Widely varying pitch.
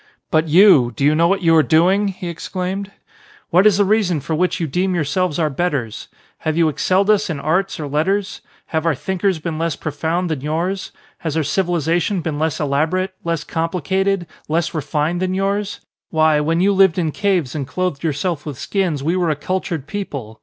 No: average, 3.5 semitones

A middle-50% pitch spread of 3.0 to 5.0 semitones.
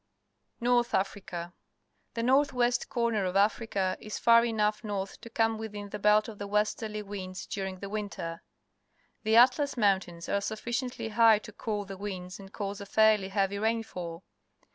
No: narrow, 2.5 semitones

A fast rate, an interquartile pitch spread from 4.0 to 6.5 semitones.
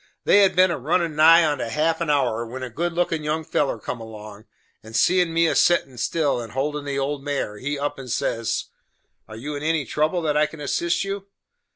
Yes: fast, 220 wpm; average, 4.5 semitones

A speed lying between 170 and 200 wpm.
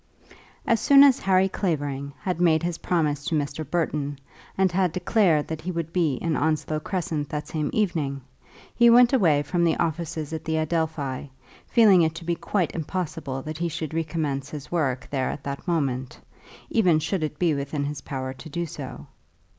Yes: average, 190 wpm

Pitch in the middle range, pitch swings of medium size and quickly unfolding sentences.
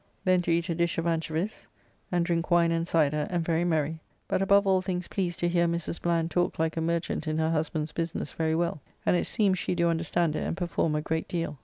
No: medium, 170 Hz; narrow, 1.4 semitones; fast, 235 wpm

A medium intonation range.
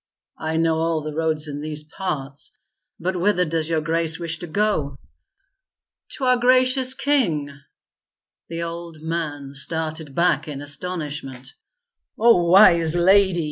Yes: average, 3.0 semitones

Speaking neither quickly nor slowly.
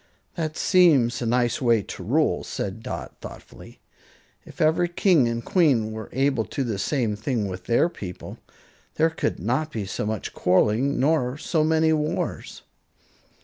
Yes: average, 160 wpm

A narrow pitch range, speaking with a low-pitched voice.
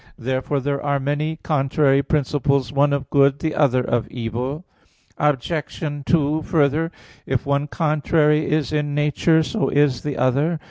No: narrow, 1.9 semitones; medium, 145 Hz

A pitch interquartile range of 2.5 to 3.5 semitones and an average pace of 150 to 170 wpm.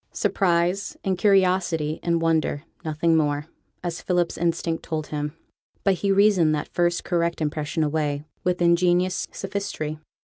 No: average, 2.8 semitones; slow, 135 wpm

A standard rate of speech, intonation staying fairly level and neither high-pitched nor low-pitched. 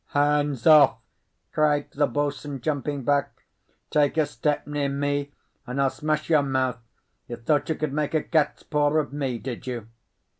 Yes: average, 165 wpm; narrow, 1.5 semitones; medium, 145 Hz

